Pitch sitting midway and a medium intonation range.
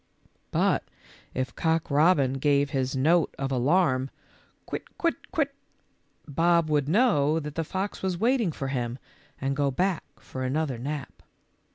Yes: medium, 150 Hz; average, 4.3 semitones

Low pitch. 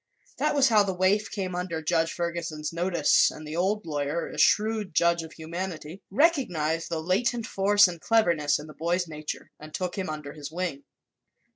No: medium, 170 Hz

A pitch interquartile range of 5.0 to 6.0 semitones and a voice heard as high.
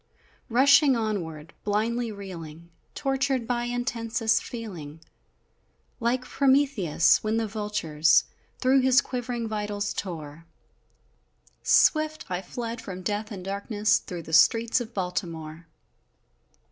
Yes: average, 5.3 semitones; high, 215 Hz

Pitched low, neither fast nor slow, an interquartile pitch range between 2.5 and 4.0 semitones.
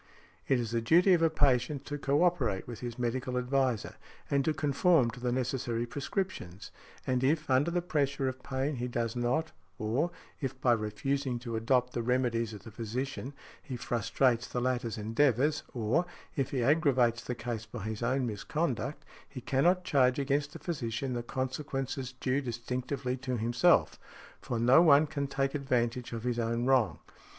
Yes: low, 130 Hz; average, 175 wpm; average, 2.9 semitones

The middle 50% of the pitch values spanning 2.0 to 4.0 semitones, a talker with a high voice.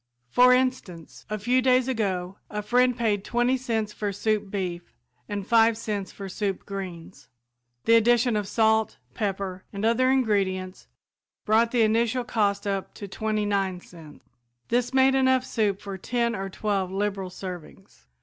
Yes: average, 3.5 semitones; high, 210 Hz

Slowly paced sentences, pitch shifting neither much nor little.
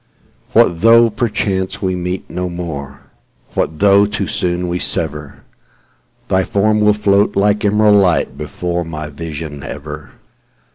Yes: slow, 115 wpm; average, 3.9 semitones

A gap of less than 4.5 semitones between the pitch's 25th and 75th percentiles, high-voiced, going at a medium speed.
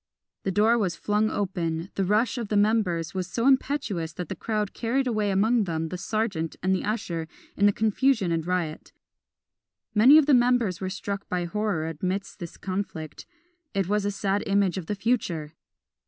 Yes: average, 3.7 semitones; high, 200 Hz; average, 185 wpm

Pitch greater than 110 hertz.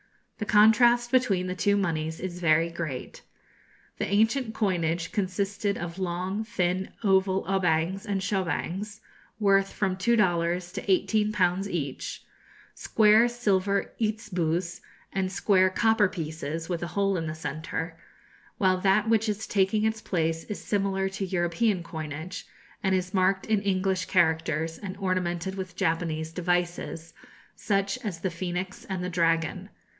Yes: medium, 185 Hz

